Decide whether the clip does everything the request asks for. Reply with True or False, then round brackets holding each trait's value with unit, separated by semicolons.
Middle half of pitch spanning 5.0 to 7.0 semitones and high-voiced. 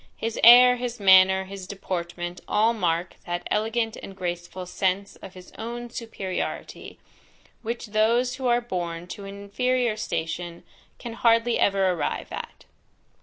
False (4.2 semitones; 200 Hz)